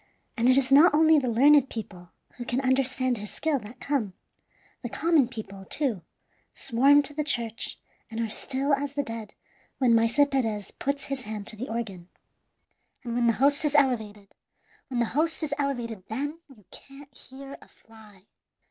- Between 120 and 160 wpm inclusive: No, average, 175 wpm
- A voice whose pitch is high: Yes, very high, 255 Hz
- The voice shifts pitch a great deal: No, average, 3.9 semitones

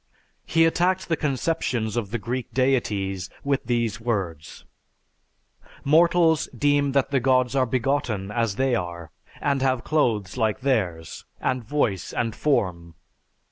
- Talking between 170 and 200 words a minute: No, slow, 135 wpm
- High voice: No, low, 125 Hz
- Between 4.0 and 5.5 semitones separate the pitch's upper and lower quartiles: Yes, average, 5.2 semitones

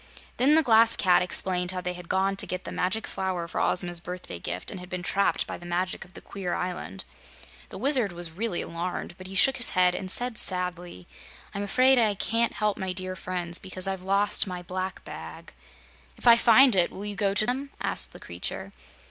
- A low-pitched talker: No, medium, 185 Hz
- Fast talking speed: Yes, fast, 215 wpm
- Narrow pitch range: No, average, 3.0 semitones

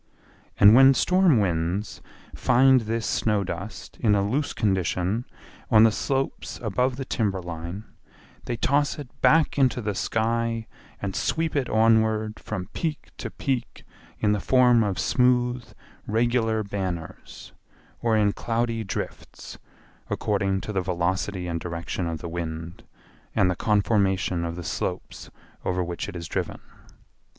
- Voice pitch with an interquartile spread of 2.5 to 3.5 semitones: No, average, 4.6 semitones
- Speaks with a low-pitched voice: Yes, low, 105 Hz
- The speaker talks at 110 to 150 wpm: Yes, average, 140 wpm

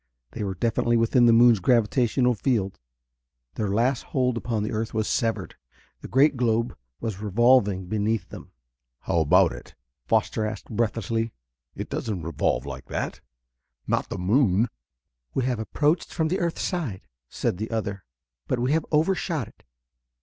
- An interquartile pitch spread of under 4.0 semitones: Yes, average, 3.5 semitones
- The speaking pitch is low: Yes, low, 115 Hz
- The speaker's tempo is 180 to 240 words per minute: No, average, 155 wpm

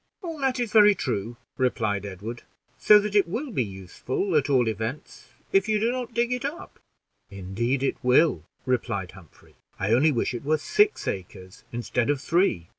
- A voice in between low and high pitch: No, low, 130 Hz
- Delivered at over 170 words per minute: Yes, average, 180 wpm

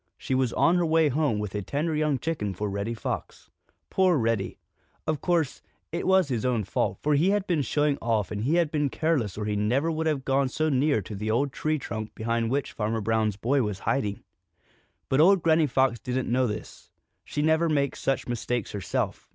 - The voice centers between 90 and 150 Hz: Yes, low, 135 Hz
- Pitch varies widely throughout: Yes, wide, 5.9 semitones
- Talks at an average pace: No, fast, 210 wpm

